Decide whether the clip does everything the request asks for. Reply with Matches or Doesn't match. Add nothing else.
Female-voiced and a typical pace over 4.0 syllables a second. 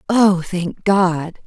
Doesn't match